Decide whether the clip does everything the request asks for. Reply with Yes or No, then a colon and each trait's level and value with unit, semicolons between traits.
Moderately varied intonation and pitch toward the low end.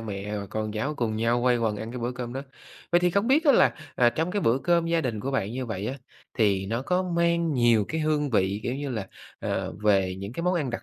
No: wide, 6.9 semitones; low, 120 Hz